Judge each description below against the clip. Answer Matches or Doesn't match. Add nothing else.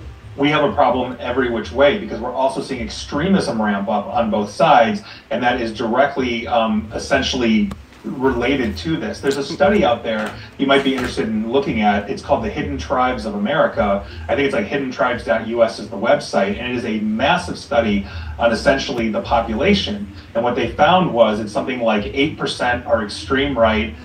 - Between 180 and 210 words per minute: Matches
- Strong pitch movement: Doesn't match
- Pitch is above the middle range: Doesn't match